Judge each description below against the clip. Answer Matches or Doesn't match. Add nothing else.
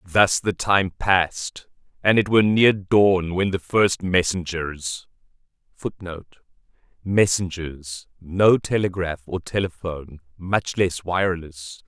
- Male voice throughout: Matches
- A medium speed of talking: Doesn't match